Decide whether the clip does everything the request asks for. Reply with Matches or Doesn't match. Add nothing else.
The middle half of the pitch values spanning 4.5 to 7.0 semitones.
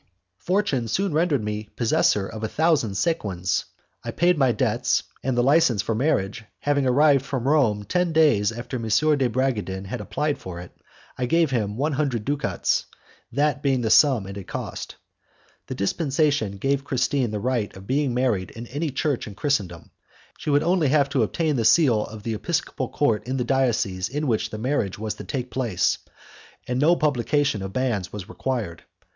Matches